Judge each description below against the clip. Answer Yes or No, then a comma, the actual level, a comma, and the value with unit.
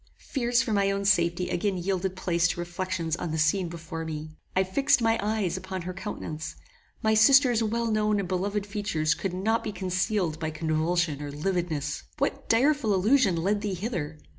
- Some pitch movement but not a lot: Yes, average, 4.0 semitones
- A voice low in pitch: No, high, 190 Hz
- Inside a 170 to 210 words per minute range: Yes, average, 180 wpm